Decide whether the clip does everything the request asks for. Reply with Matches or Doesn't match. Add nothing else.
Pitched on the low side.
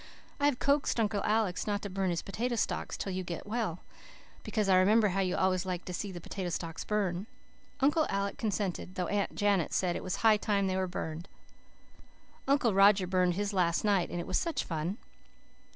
Doesn't match